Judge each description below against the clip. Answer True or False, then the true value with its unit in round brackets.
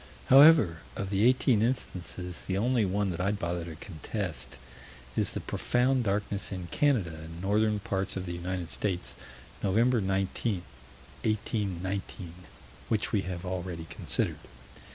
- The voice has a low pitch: True (95 Hz)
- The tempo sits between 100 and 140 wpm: True (135 wpm)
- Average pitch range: True (3.4 semitones)